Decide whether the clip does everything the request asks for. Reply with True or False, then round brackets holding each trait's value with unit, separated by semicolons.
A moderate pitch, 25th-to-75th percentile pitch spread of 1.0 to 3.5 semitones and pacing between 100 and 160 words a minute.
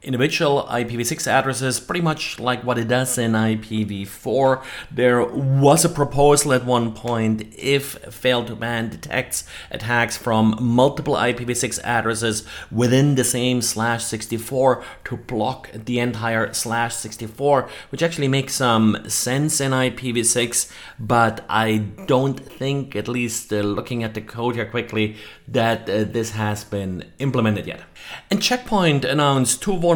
False (120 Hz; 3.1 semitones; 145 wpm)